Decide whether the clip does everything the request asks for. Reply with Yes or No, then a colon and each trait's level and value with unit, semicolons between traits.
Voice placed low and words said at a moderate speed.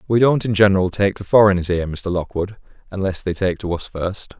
No: very low, 95 Hz; fast, 220 wpm